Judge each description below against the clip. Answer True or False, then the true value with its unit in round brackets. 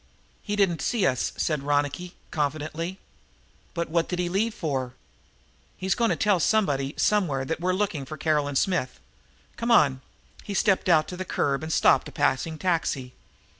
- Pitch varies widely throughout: False (4.7 semitones)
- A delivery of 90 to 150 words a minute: False (170 wpm)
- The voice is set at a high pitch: False (165 Hz)